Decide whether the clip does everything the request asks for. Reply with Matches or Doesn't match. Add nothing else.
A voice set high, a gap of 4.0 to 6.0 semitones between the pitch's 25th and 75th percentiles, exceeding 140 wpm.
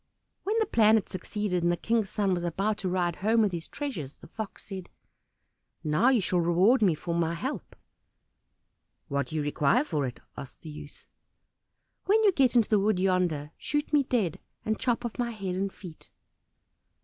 Matches